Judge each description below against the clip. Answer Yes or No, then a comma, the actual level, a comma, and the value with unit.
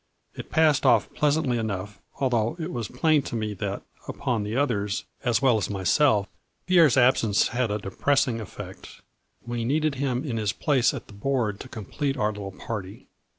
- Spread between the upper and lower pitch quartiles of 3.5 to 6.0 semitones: Yes, average, 4.9 semitones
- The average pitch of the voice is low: Yes, low, 120 Hz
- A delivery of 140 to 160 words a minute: No, average, 180 wpm